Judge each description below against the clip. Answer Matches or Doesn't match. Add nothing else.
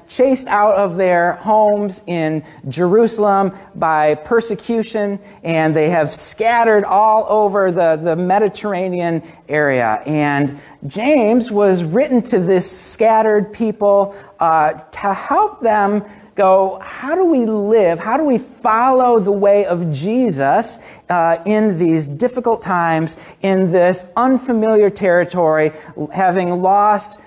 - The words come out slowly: Matches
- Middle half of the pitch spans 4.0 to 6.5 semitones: Matches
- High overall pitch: Matches